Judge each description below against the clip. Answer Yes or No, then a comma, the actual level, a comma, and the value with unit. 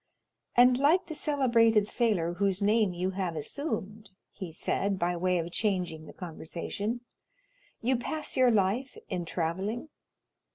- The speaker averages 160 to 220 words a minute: No, slow, 135 wpm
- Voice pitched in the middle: No, high, 200 Hz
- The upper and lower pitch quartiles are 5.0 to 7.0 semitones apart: Yes, average, 5.3 semitones